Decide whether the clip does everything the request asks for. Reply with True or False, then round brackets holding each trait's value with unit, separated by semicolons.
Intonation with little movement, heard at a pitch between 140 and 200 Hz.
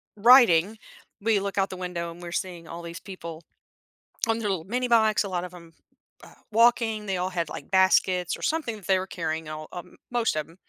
False (4.2 semitones; 185 Hz)